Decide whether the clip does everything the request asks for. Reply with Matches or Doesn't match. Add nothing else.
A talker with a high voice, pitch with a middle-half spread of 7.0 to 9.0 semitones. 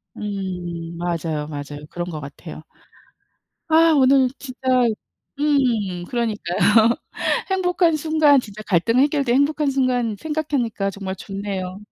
Matches